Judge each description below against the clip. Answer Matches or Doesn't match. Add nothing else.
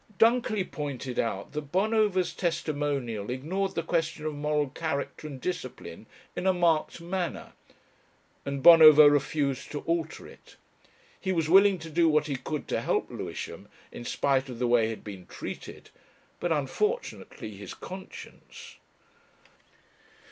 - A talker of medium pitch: Matches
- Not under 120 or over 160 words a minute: Matches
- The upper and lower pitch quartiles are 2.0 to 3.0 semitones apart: Doesn't match